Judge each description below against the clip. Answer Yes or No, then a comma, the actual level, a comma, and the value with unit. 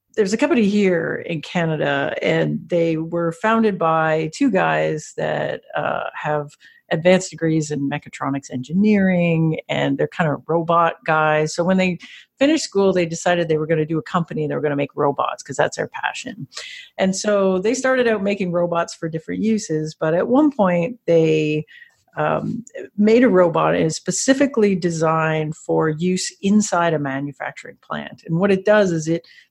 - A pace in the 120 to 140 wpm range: No, average, 175 wpm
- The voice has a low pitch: No, medium, 170 Hz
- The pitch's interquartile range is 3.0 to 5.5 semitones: Yes, average, 4.2 semitones